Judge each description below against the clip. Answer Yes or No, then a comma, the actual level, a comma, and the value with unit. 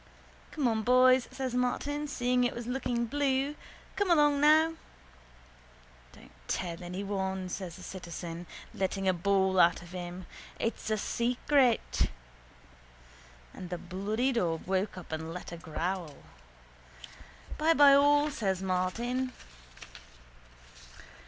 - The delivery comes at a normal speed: No, slow, 120 wpm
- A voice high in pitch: Yes, high, 215 Hz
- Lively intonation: Yes, wide, 6.2 semitones